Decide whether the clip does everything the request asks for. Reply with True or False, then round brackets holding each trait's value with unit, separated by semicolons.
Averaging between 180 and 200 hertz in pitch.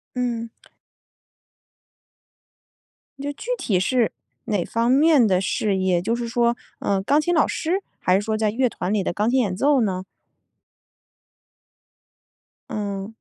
False (225 Hz)